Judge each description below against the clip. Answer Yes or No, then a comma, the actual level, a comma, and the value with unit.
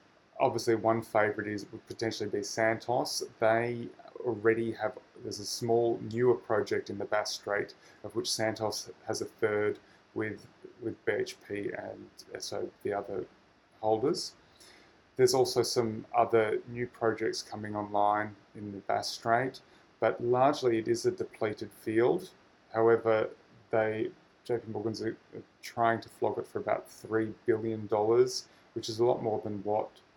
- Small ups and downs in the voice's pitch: Yes, narrow, 2.3 semitones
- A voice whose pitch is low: Yes, low, 115 Hz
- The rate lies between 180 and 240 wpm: No, average, 145 wpm